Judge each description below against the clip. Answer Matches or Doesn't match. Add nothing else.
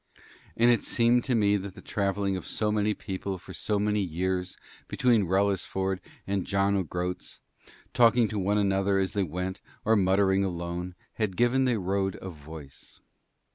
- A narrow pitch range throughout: Matches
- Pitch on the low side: Matches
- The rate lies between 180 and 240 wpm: Doesn't match